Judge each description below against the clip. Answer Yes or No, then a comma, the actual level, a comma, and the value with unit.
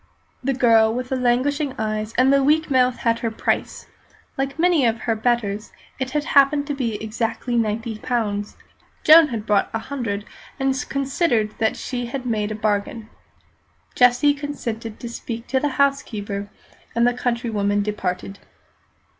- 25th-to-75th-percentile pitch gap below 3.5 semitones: No, average, 3.9 semitones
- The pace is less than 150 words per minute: No, average, 155 wpm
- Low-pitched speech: No, high, 240 Hz